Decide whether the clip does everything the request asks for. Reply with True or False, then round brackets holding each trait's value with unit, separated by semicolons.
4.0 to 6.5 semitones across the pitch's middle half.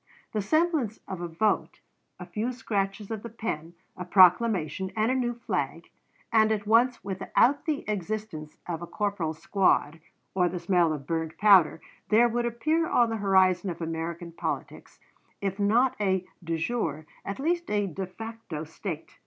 True (4.8 semitones)